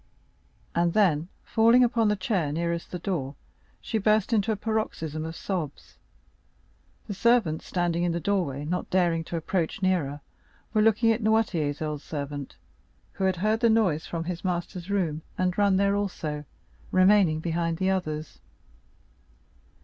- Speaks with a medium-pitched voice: Yes, medium, 180 Hz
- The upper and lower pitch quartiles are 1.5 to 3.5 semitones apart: No, average, 4.2 semitones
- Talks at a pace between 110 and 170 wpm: Yes, average, 150 wpm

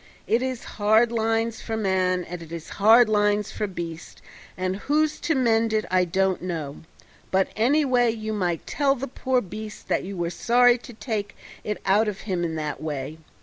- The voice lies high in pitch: Yes, high, 210 Hz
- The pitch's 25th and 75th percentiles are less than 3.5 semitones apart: No, average, 4.2 semitones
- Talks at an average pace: Yes, average, 190 wpm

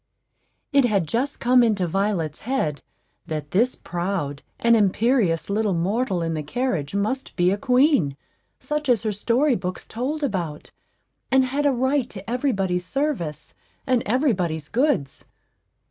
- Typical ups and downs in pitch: No, wide, 6.8 semitones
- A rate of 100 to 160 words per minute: Yes, average, 150 wpm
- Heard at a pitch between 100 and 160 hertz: No, high, 210 Hz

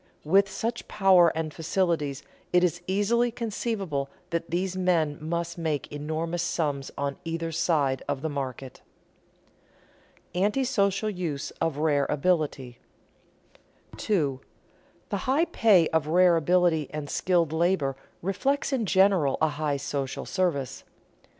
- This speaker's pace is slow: Yes, slow, 125 wpm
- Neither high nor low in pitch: Yes, medium, 165 Hz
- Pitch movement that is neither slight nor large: Yes, average, 4.5 semitones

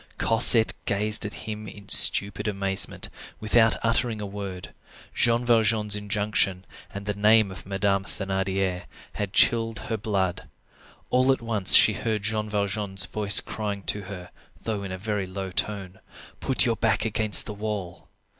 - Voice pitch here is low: Yes, low, 105 Hz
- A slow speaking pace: No, average, 155 wpm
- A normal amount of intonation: No, narrow, 2.1 semitones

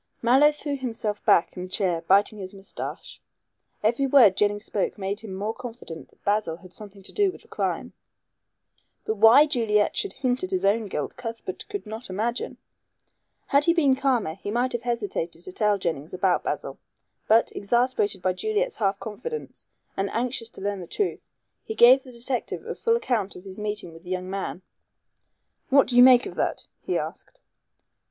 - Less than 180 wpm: No, average, 185 wpm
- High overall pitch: Yes, high, 220 Hz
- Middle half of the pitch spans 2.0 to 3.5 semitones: No, average, 4.7 semitones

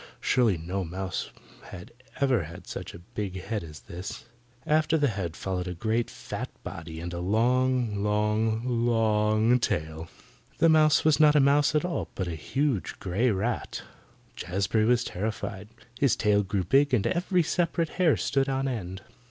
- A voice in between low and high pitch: No, low, 110 Hz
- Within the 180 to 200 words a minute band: No, average, 165 wpm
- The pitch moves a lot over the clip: Yes, wide, 6.3 semitones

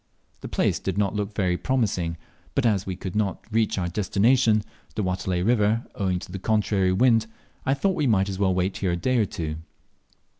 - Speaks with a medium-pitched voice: No, low, 100 Hz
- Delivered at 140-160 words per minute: No, average, 200 wpm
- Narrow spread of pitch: No, average, 3.3 semitones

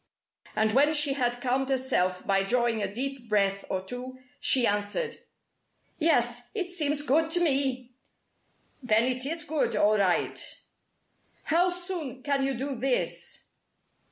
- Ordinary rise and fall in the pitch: Yes, average, 4.2 semitones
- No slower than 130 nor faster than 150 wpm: Yes, average, 140 wpm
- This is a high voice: Yes, very high, 255 Hz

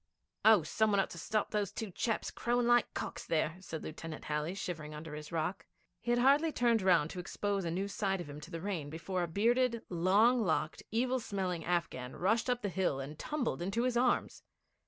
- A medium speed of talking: No, fast, 215 wpm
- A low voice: No, high, 190 Hz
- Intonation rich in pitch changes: Yes, wide, 5.9 semitones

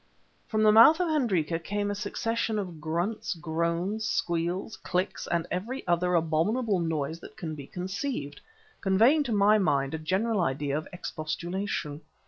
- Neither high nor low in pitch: Yes, medium, 180 Hz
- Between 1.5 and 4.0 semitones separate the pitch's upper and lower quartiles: No, average, 4.8 semitones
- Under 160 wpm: Yes, average, 150 wpm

